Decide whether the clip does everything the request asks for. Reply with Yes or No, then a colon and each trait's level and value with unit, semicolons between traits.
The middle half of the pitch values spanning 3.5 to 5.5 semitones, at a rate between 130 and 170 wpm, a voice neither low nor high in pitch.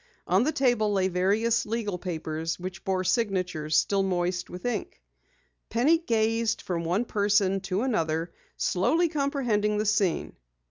No: average, 4.3 semitones; average, 140 wpm; high, 200 Hz